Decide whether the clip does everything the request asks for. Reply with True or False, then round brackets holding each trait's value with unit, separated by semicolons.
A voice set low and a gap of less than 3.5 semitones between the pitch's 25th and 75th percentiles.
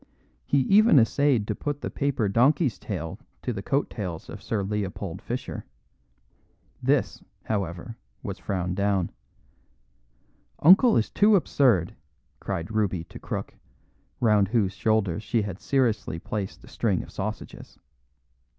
False (105 Hz; 4.8 semitones)